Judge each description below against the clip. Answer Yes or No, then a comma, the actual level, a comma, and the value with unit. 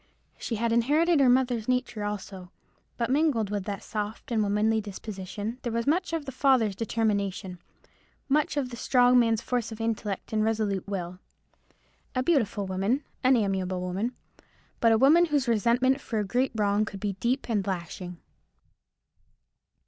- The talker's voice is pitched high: Yes, high, 225 Hz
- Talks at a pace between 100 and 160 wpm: Yes, average, 155 wpm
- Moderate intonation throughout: Yes, average, 3.9 semitones